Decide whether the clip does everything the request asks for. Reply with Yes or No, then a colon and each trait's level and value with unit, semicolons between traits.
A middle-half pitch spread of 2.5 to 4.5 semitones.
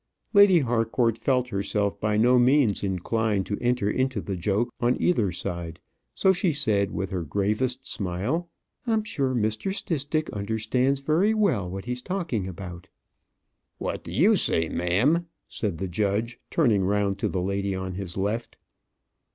No: average, 5.3 semitones